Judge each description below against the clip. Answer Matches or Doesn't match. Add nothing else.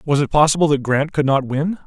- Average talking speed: Doesn't match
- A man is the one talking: Matches